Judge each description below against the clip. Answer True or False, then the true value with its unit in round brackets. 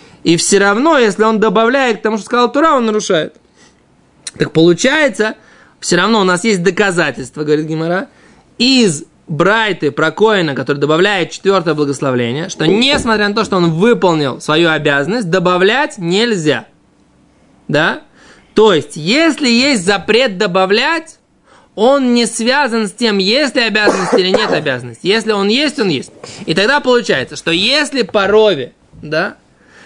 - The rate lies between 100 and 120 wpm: False (145 wpm)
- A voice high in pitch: True (205 Hz)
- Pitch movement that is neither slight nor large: False (6.0 semitones)